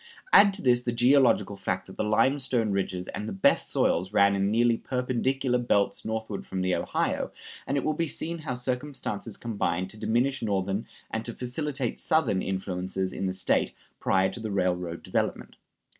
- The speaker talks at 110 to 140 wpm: No, average, 175 wpm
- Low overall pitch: Yes, low, 110 Hz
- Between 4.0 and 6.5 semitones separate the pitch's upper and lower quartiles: Yes, average, 4.9 semitones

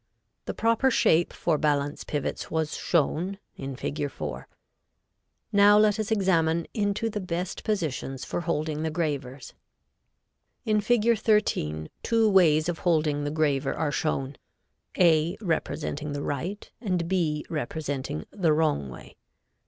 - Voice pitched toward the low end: No, medium, 160 Hz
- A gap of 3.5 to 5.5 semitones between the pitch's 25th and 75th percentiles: Yes, average, 5.2 semitones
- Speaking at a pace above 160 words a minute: No, slow, 135 wpm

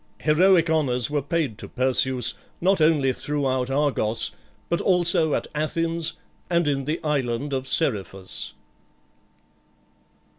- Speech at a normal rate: No, slow, 115 wpm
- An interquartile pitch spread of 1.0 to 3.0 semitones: No, average, 4.1 semitones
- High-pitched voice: No, medium, 145 Hz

